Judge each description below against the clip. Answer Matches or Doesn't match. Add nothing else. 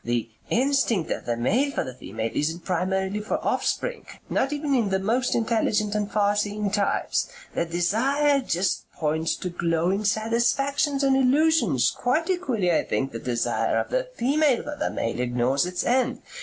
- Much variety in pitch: Matches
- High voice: Matches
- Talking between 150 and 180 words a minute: Matches